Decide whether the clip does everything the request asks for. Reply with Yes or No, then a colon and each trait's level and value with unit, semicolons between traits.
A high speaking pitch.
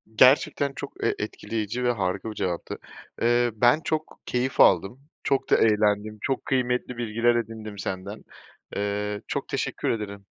No: low, 110 Hz